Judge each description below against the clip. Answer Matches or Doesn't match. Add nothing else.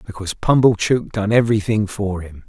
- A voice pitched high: Doesn't match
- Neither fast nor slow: Matches